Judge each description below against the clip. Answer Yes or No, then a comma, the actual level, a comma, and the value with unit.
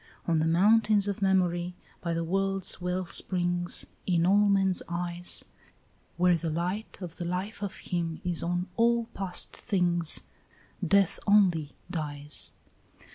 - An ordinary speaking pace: No, slow, 130 wpm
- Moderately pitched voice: Yes, medium, 180 Hz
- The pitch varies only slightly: Yes, narrow, 2.3 semitones